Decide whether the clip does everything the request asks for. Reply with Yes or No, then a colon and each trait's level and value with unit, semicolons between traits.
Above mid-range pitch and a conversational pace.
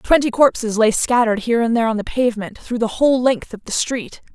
No: high, 235 Hz; fast, 235 wpm